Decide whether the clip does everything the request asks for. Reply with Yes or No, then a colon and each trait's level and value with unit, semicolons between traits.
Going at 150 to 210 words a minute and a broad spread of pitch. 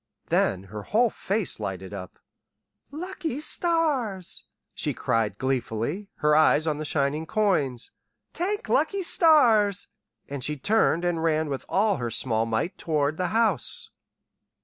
No: slow, 135 wpm; wide, 9.0 semitones